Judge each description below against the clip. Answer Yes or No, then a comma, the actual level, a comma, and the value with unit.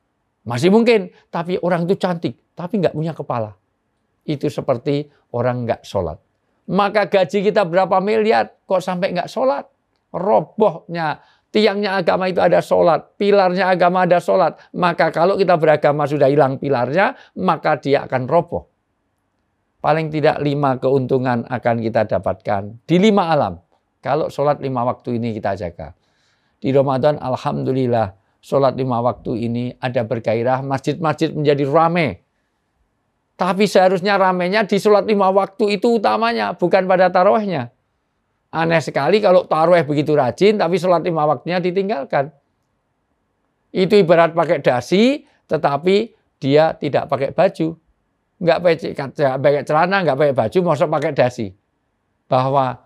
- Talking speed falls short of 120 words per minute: No, average, 130 wpm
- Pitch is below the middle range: No, medium, 150 Hz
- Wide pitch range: Yes, wide, 7.1 semitones